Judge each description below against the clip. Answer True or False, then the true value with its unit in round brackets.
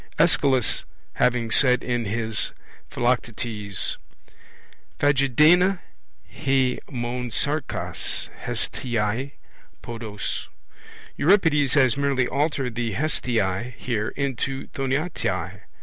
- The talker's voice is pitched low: True (125 Hz)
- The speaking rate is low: True (80 wpm)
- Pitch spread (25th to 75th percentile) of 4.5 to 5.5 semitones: False (3.3 semitones)